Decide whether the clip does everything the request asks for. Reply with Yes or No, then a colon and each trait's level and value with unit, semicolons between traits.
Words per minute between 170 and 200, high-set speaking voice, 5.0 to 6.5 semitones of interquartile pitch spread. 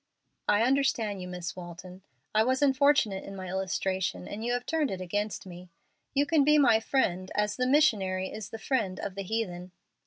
Yes: average, 190 wpm; high, 205 Hz; wide, 5.5 semitones